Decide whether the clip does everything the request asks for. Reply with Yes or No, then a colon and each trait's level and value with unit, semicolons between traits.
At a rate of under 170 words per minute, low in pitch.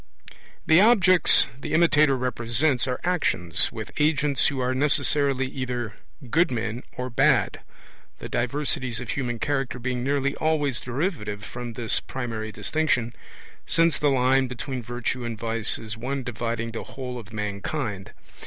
Yes: average, 145 wpm; low, 125 Hz